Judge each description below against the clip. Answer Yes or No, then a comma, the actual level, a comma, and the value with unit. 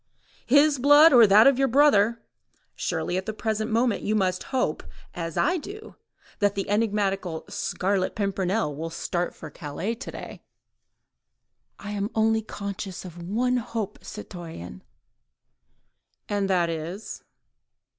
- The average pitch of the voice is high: Yes, high, 205 Hz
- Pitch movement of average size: Yes, average, 4.2 semitones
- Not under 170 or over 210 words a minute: No, slow, 135 wpm